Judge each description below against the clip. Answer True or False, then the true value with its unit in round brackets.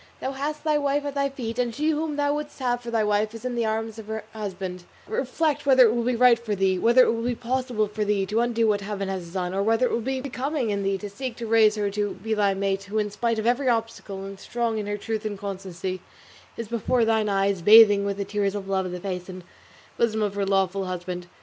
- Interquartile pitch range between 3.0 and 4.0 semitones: True (3.5 semitones)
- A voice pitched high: True (220 Hz)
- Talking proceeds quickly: True (260 wpm)